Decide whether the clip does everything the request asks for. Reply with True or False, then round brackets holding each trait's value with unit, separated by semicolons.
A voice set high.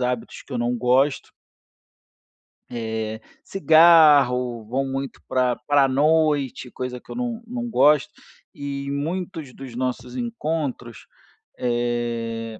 False (135 Hz)